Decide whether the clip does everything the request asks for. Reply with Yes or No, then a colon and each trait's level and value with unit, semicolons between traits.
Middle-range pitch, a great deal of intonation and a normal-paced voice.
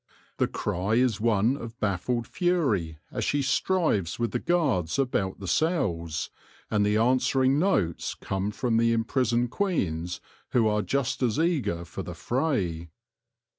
No: low, 115 Hz; wide, 5.9 semitones; average, 145 wpm